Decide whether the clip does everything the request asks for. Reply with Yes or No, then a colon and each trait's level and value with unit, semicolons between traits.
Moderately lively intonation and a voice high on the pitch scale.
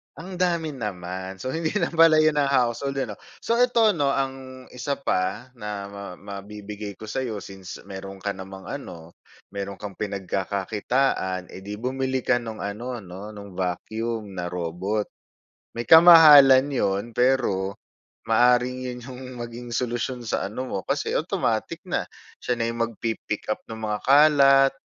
No: average, 5.0 semitones; low, 115 Hz